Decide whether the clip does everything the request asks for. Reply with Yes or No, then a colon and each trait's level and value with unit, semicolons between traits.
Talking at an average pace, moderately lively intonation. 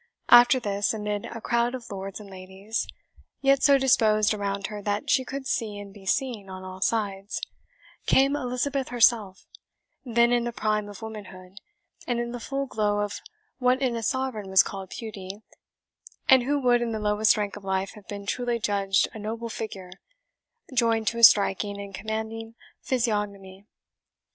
Yes: average, 170 wpm; average, 3.1 semitones